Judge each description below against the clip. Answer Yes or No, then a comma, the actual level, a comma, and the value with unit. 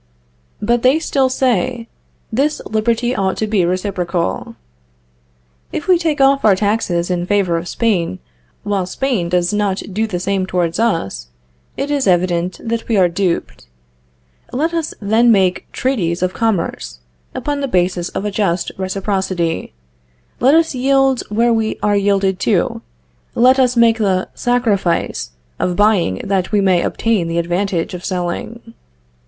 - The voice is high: Yes, high, 200 Hz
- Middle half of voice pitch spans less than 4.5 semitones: No, average, 4.9 semitones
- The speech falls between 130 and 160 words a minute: Yes, average, 150 wpm